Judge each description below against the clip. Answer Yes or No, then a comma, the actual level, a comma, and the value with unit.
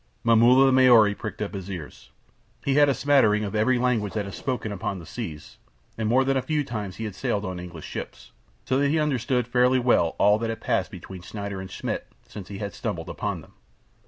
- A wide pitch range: No, average, 4.3 semitones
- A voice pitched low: Yes, low, 110 Hz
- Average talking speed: No, fast, 220 wpm